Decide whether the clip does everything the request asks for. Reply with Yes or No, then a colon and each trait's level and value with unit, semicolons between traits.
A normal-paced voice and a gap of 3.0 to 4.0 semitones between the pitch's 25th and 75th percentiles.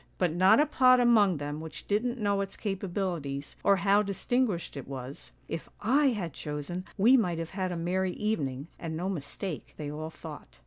No: average, 195 wpm; average, 4.7 semitones